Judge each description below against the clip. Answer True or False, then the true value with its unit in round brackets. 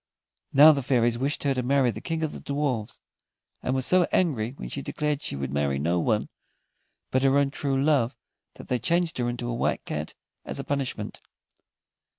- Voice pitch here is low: True (130 Hz)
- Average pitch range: True (3.6 semitones)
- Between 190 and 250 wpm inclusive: True (195 wpm)